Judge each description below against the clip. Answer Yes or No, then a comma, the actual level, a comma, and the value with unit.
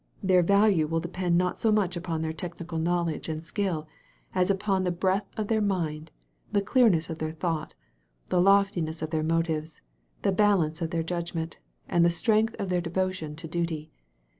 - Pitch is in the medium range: Yes, medium, 175 Hz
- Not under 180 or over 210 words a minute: Yes, average, 185 wpm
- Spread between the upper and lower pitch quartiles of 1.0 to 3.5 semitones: Yes, average, 2.9 semitones